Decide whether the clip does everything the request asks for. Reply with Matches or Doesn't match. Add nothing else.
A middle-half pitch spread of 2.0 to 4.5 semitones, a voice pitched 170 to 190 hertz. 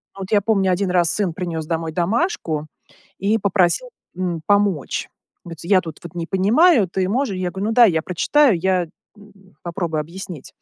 Matches